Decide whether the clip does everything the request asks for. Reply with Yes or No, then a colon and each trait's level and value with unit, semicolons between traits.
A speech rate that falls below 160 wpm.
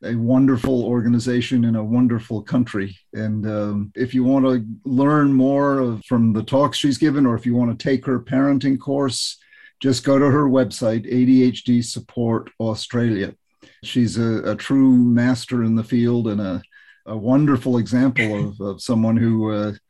No: average, 170 wpm